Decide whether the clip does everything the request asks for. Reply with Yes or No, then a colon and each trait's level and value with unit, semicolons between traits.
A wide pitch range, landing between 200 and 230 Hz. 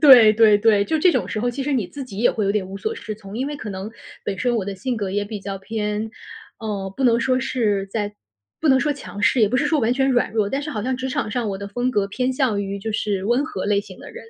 No: average, 4.1 semitones; high, 220 Hz